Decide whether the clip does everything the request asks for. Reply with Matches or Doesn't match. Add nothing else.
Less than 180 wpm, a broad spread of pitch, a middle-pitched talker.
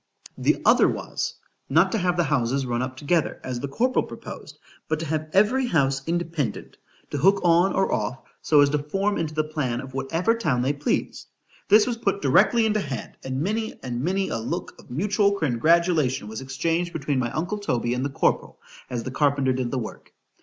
Doesn't match